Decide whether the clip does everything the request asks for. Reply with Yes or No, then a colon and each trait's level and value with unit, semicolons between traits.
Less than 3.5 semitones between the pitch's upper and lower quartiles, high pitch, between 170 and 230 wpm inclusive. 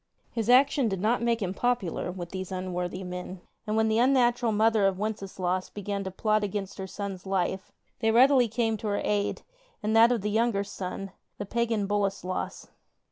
Yes: average, 3.0 semitones; high, 205 Hz; average, 190 wpm